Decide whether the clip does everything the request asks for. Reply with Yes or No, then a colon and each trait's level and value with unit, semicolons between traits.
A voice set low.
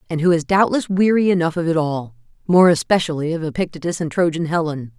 No: medium, 165 Hz